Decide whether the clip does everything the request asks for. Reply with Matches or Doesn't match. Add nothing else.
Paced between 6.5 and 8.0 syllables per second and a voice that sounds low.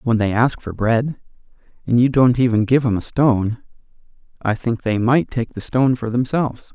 Doesn't match